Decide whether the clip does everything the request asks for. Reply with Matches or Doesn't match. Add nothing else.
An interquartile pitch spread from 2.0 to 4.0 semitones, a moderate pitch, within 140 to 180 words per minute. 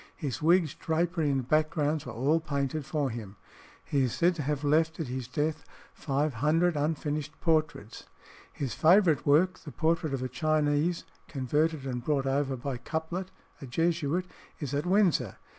Matches